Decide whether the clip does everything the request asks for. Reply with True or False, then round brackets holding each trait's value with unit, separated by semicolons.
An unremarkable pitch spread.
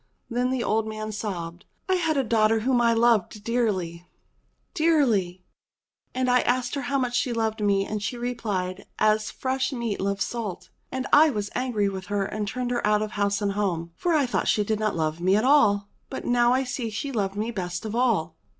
True (3.6 semitones)